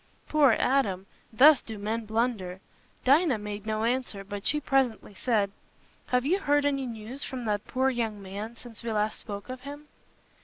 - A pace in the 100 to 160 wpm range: No, average, 175 wpm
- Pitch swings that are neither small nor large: Yes, average, 4.2 semitones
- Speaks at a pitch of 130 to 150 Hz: No, high, 230 Hz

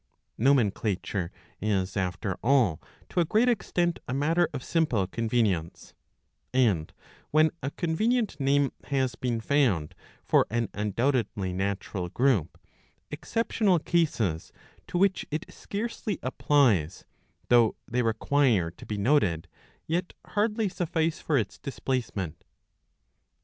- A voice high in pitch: No, low, 125 Hz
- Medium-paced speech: No, slow, 115 wpm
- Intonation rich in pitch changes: Yes, wide, 8.1 semitones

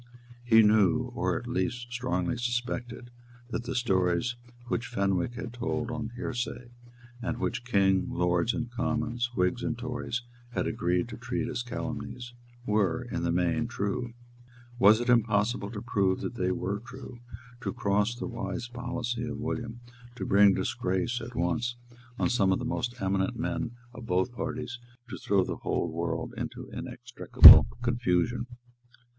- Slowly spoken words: No, average, 155 wpm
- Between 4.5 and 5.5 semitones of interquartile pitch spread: No, average, 3.6 semitones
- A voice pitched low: Yes, low, 115 Hz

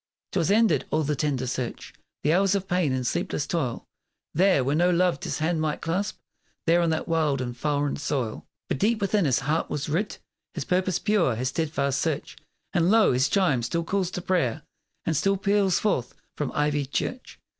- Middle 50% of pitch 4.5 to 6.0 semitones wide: Yes, average, 5.0 semitones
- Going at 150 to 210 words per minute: Yes, average, 190 wpm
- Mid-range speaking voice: Yes, medium, 160 Hz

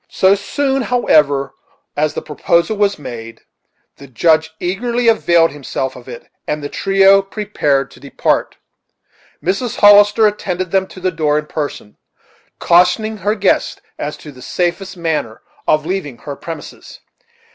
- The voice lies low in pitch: No, medium, 175 Hz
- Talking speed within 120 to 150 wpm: Yes, average, 145 wpm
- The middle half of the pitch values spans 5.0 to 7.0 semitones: Yes, wide, 5.5 semitones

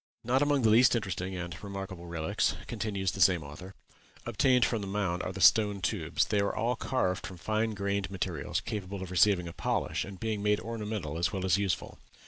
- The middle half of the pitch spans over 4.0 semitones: No, average, 3.0 semitones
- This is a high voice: No, low, 100 Hz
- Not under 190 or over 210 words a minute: Yes, average, 200 wpm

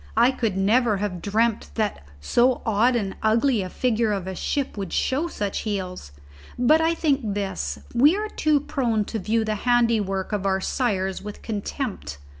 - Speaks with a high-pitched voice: Yes, high, 220 Hz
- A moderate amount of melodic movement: Yes, average, 4.1 semitones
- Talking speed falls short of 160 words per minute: No, average, 175 wpm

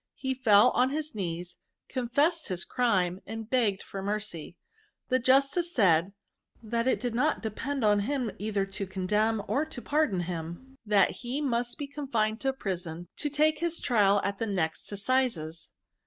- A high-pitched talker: Yes, high, 225 Hz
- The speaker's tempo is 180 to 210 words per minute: No, average, 170 wpm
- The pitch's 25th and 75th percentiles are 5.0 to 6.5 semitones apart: Yes, wide, 5.4 semitones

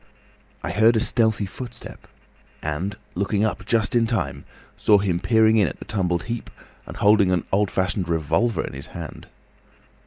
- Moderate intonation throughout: Yes, average, 4.2 semitones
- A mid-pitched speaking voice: No, low, 100 Hz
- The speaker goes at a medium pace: Yes, average, 165 wpm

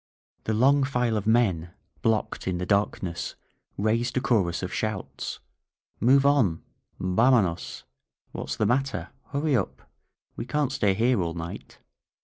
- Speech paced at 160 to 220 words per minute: No, slow, 135 wpm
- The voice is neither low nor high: No, low, 110 Hz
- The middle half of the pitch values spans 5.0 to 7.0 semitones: Yes, wide, 5.6 semitones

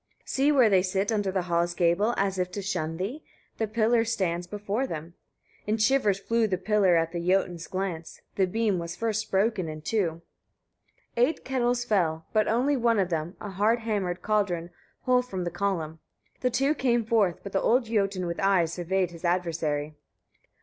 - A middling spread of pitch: Yes, average, 4.5 semitones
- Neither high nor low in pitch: No, high, 195 Hz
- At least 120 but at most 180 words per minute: No, average, 190 wpm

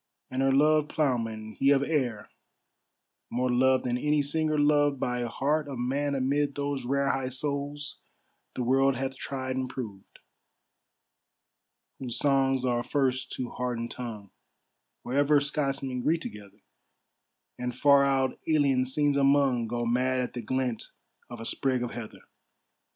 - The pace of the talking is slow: No, average, 145 wpm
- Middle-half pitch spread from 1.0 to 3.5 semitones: Yes, narrow, 2.4 semitones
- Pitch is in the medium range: No, low, 130 Hz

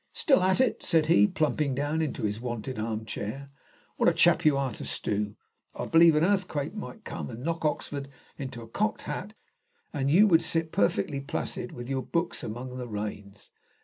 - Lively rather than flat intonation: Yes, wide, 6.0 semitones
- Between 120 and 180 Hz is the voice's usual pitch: Yes, medium, 140 Hz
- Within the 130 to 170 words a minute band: No, average, 190 wpm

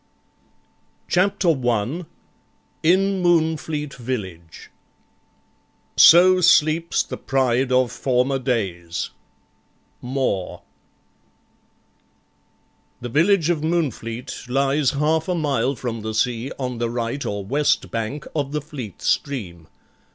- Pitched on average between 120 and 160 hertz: Yes, low, 135 Hz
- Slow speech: Yes, slow, 100 wpm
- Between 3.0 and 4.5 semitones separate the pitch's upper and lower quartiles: No, average, 5.1 semitones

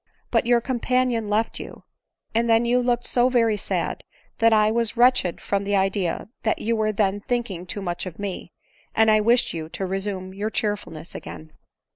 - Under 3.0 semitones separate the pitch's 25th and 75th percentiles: No, average, 3.4 semitones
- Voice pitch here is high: Yes, high, 215 Hz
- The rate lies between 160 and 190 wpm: Yes, average, 185 wpm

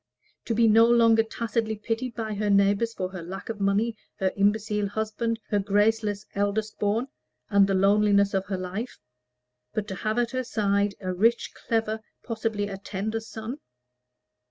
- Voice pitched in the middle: No, high, 210 Hz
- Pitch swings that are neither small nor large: No, narrow, 2.1 semitones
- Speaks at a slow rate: No, average, 165 wpm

